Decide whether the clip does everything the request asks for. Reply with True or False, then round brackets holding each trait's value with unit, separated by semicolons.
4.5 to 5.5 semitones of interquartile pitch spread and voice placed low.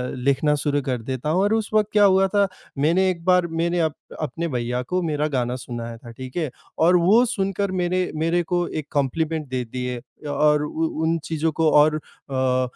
False (5.2 semitones; 155 Hz)